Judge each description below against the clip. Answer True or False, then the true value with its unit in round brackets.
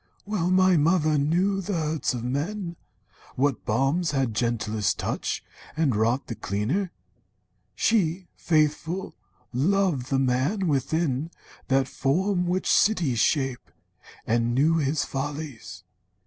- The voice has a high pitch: False (150 Hz)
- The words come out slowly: True (120 wpm)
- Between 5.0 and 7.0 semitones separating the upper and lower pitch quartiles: True (5.6 semitones)